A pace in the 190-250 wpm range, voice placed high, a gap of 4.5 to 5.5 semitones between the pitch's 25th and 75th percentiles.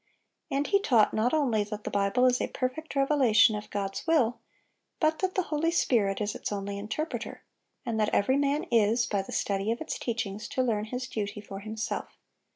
Yes: average, 195 wpm; high, 230 Hz; average, 5.0 semitones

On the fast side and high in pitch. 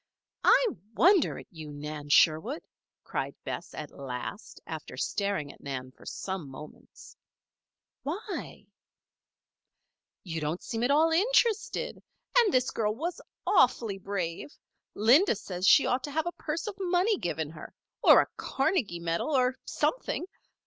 No: average, 140 wpm; high, 215 Hz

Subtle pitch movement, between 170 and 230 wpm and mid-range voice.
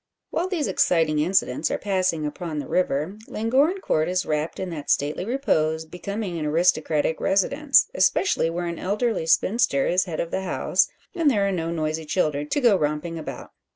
No: average, 4.6 semitones; average, 180 wpm; medium, 175 Hz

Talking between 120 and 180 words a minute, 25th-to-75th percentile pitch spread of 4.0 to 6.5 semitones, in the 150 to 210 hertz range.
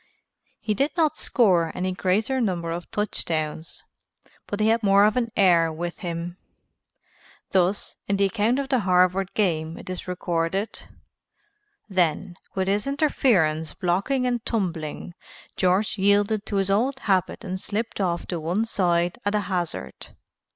No: average, 150 wpm; average, 3.6 semitones; high, 190 Hz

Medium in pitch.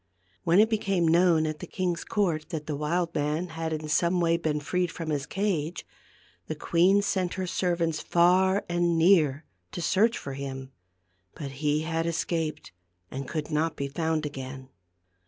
Yes: medium, 165 Hz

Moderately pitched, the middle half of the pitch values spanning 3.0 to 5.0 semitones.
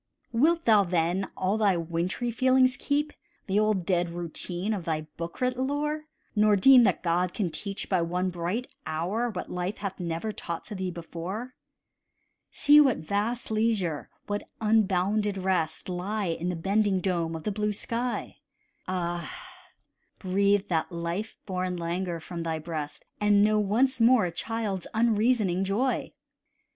No: high, 195 Hz; average, 4.1 semitones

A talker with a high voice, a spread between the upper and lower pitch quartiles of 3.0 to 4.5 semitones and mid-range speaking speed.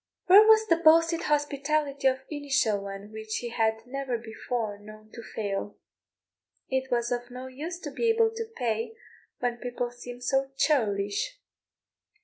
No: very high, 250 Hz; average, 5.2 semitones; average, 150 wpm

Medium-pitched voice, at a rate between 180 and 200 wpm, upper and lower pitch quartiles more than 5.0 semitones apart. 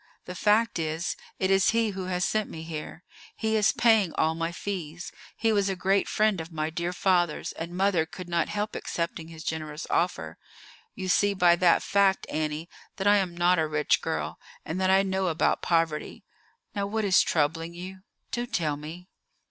No: medium, 180 Hz; average, 190 wpm; average, 3.2 semitones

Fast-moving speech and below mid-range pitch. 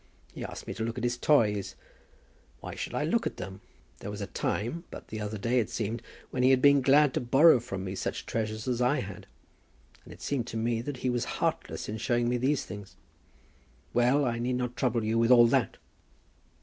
Yes: fast, 220 wpm; low, 120 Hz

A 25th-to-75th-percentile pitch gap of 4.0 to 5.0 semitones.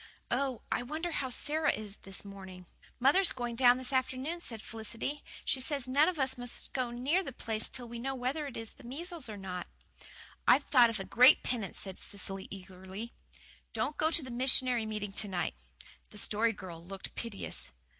Yes: average, 4.7 semitones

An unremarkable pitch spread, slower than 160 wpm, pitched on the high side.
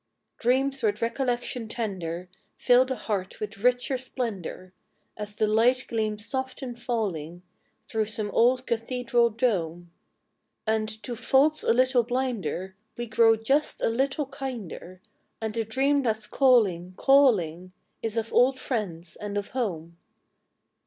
Yes: average, 4.0 semitones; average, 140 wpm; high, 225 Hz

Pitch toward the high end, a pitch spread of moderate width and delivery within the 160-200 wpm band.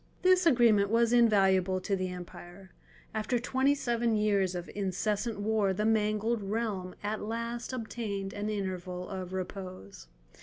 No: high, 210 Hz; average, 3.4 semitones; average, 140 wpm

